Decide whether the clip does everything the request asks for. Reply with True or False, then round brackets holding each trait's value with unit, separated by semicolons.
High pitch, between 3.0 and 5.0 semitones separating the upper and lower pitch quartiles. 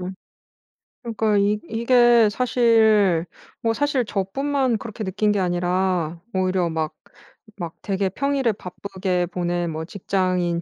True (195 Hz; 4.1 semitones)